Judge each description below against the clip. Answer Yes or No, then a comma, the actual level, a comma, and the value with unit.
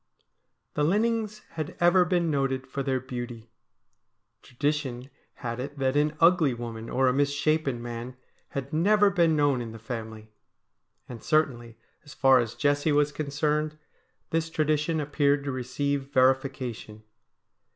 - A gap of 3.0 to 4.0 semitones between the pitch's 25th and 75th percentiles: Yes, average, 3.6 semitones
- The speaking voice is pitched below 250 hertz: Yes, medium, 140 Hz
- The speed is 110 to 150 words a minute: Yes, average, 140 wpm